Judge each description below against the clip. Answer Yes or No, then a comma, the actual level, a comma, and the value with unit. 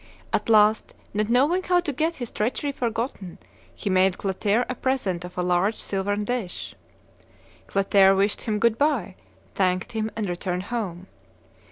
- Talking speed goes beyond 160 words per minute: No, average, 155 wpm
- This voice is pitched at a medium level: No, high, 210 Hz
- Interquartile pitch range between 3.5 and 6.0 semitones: Yes, average, 4.3 semitones